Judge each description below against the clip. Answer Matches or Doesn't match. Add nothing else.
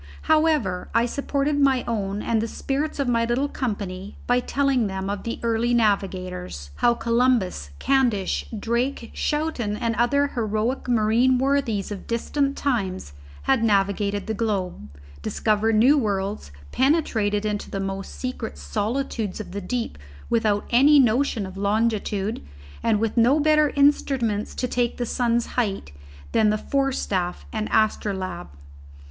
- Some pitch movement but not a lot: Matches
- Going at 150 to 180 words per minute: Doesn't match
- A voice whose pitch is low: Doesn't match